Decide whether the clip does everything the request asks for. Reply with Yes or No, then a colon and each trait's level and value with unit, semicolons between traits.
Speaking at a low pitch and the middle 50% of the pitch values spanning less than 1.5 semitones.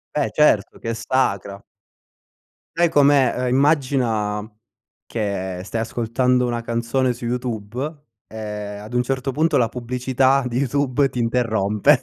No: low, 125 Hz; average, 2.9 semitones